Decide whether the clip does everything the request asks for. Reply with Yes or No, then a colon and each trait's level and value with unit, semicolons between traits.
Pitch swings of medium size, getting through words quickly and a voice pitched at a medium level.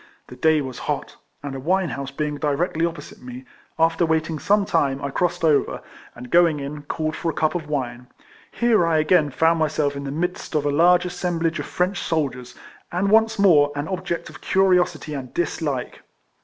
No: average, 3.6 semitones; average, 195 wpm; medium, 160 Hz